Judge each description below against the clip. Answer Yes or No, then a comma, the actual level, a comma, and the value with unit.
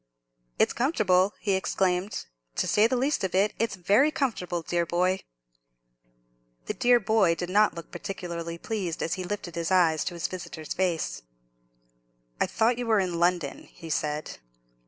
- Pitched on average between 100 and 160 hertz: No, medium, 185 Hz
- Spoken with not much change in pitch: No, average, 3.8 semitones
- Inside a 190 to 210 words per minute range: No, average, 160 wpm